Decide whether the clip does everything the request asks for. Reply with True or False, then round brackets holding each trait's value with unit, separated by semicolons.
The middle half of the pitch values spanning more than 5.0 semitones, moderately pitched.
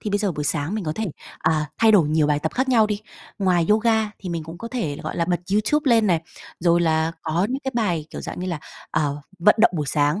True (5.4 semitones; 175 Hz)